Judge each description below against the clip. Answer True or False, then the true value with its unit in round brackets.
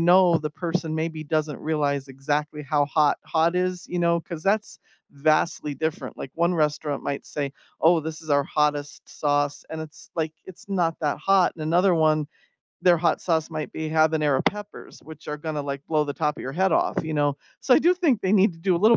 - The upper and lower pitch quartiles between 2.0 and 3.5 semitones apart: True (2.7 semitones)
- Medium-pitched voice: True (155 Hz)